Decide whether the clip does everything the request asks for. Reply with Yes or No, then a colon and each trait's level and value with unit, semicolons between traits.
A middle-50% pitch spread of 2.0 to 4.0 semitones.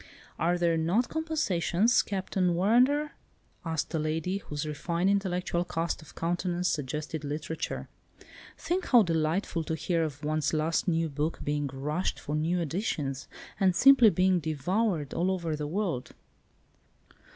Yes: average, 3.5 semitones